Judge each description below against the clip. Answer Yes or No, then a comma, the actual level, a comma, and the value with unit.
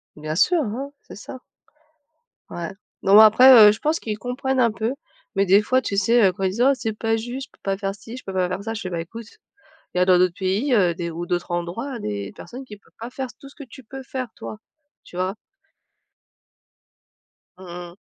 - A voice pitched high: Yes, high, 215 Hz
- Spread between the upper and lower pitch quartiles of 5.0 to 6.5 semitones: Yes, wide, 5.4 semitones